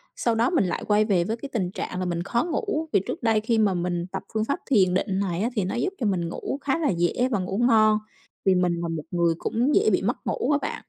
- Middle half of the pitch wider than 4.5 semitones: Yes, average, 4.9 semitones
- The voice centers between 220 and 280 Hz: No, high, 210 Hz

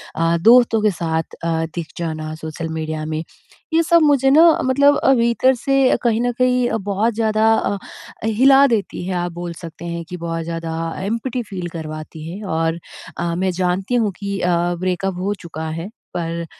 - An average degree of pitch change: No, wide, 5.8 semitones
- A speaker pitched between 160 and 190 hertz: Yes, medium, 185 Hz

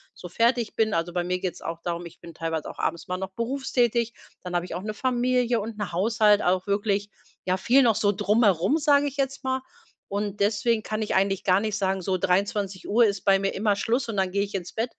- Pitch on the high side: Yes, high, 205 Hz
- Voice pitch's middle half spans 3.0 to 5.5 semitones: Yes, average, 3.7 semitones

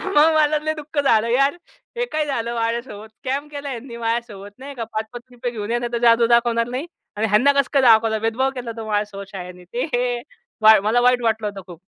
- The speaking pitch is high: Yes, high, 235 Hz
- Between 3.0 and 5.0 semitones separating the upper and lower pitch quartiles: Yes, average, 3.3 semitones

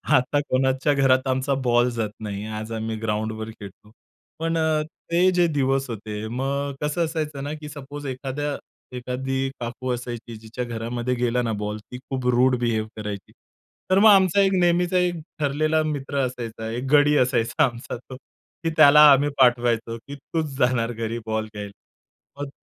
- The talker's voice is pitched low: Yes, low, 130 Hz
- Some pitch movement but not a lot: Yes, average, 4.1 semitones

